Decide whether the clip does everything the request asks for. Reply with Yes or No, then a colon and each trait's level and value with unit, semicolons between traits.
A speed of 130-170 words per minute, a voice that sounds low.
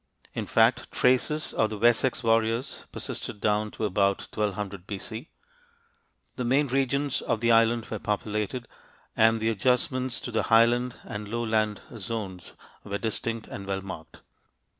Yes: average, 140 wpm; low, 115 Hz